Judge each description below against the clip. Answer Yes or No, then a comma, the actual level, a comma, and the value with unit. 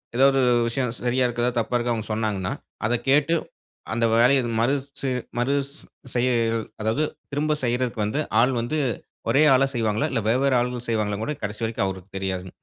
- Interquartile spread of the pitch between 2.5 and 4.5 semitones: Yes, average, 3.5 semitones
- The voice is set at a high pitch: No, low, 120 Hz